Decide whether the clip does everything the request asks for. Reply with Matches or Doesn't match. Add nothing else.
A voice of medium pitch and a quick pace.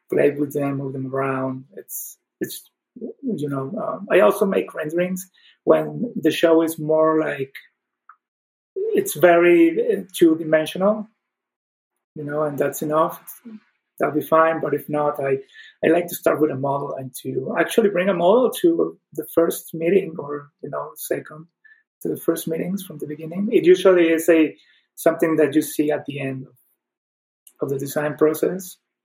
Doesn't match